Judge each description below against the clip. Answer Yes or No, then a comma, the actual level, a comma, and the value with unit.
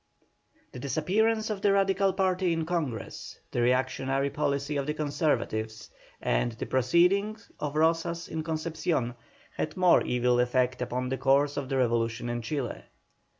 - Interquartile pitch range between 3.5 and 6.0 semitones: Yes, wide, 5.4 semitones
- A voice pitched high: No, medium, 145 Hz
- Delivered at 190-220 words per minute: No, average, 150 wpm